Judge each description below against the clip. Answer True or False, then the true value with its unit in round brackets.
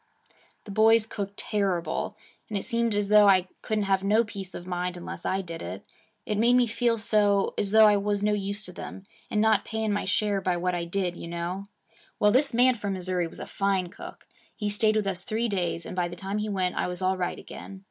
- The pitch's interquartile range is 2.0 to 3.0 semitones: True (2.7 semitones)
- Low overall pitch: False (200 Hz)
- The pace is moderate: False (235 wpm)